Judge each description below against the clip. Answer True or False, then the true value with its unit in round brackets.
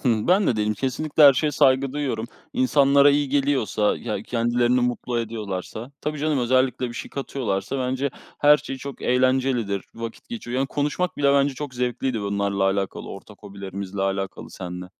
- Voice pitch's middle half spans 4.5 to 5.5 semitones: True (4.8 semitones)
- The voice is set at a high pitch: False (125 Hz)